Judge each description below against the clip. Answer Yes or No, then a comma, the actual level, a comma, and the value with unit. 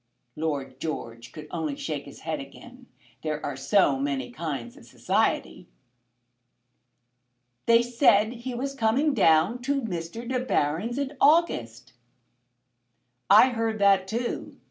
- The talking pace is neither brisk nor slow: No, slow, 125 wpm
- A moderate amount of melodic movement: No, wide, 8.9 semitones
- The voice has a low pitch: No, high, 195 Hz